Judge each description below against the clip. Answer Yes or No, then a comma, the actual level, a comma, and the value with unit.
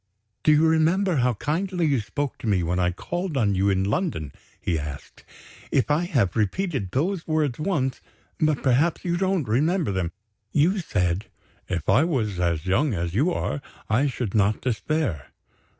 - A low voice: Yes, low, 130 Hz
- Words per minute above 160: Yes, average, 170 wpm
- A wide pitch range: Yes, wide, 8.7 semitones